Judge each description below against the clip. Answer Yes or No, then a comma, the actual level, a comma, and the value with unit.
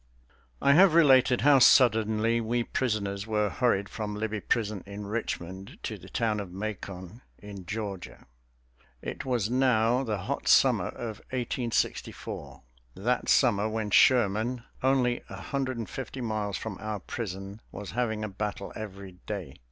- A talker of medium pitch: No, low, 110 Hz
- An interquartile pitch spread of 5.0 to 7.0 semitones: No, average, 3.3 semitones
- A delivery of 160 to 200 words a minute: No, average, 145 wpm